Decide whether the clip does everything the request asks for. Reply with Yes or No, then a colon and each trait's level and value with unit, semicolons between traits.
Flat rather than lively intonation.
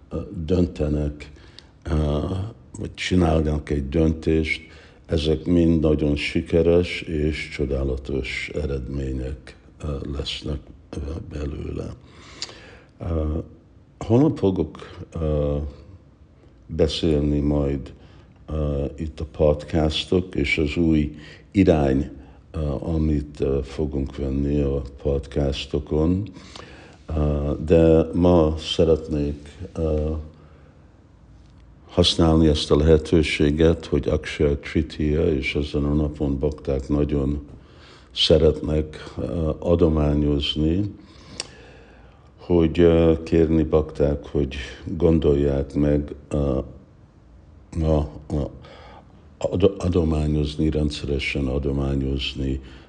Yes: narrow, 2.2 semitones